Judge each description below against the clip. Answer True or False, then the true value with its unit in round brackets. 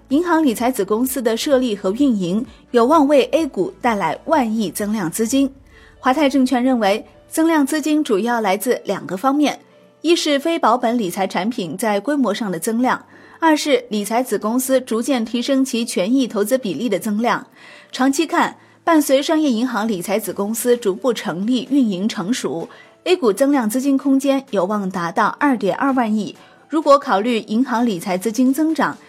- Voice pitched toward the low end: False (245 Hz)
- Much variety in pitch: False (4.4 semitones)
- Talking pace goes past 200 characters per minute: True (270 characters per minute)